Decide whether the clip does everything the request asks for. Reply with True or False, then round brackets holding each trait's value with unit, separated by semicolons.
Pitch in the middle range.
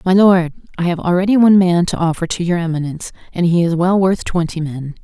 True (175 Hz)